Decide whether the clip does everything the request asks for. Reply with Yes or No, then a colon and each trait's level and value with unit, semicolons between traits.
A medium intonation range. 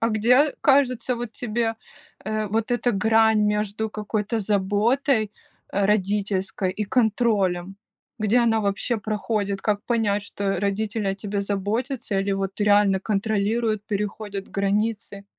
No: narrow, 2.1 semitones